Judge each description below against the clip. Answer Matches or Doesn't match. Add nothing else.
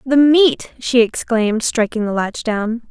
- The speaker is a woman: Matches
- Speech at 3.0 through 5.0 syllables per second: Matches